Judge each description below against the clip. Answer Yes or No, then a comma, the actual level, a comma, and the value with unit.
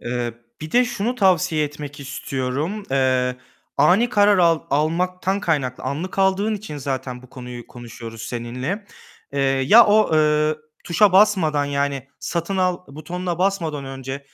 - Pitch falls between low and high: Yes, medium, 155 Hz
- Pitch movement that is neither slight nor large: No, wide, 5.8 semitones